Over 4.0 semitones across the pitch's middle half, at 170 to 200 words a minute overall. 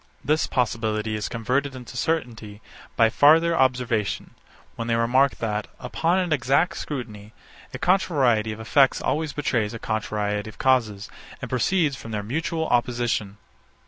No: average, 4.8 semitones; average, 145 wpm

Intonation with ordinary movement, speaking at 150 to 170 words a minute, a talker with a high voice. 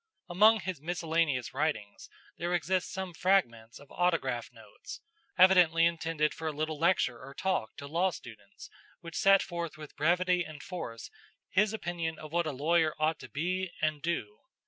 No: average, 3.6 semitones; average, 165 wpm; medium, 165 Hz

